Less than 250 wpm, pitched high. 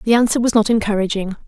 Yes: fast, 205 wpm; high, 215 Hz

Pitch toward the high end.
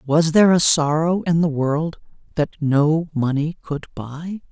No: medium, 155 Hz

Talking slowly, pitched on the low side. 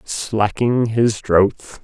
Yes: slow, 100 wpm; low, 110 Hz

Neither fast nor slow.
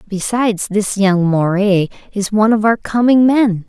Yes: average, 165 wpm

